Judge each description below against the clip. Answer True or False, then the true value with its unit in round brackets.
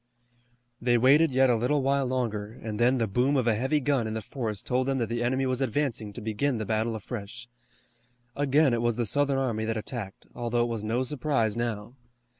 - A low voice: True (120 Hz)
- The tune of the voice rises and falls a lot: False (3.2 semitones)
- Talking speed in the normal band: False (215 wpm)